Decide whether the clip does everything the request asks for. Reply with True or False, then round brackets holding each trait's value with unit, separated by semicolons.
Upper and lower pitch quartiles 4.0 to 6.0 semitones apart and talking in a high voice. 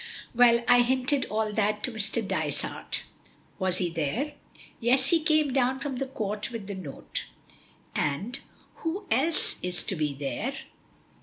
True (5.3 semitones; 235 Hz)